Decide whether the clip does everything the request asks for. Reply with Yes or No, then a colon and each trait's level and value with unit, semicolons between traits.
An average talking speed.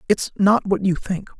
No: fast, 215 wpm